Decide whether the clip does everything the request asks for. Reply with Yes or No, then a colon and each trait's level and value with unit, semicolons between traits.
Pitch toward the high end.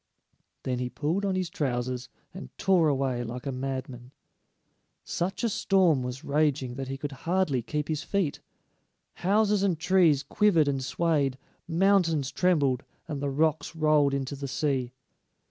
No: medium, 145 Hz